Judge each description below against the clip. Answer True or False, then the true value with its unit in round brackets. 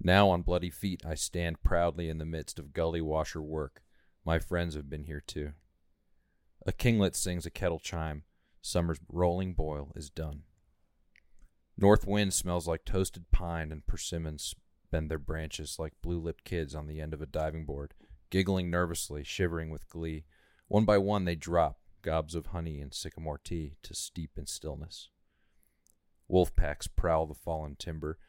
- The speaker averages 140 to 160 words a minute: False (170 wpm)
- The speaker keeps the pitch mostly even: True (2.3 semitones)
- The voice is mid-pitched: False (80 Hz)